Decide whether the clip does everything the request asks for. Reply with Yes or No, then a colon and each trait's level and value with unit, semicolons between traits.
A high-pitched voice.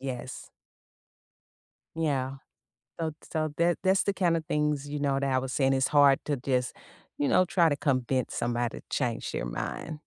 No: medium, 140 Hz